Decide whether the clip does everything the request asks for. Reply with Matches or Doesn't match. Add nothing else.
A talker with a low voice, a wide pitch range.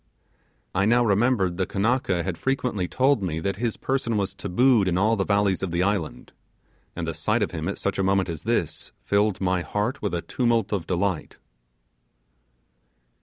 Doesn't match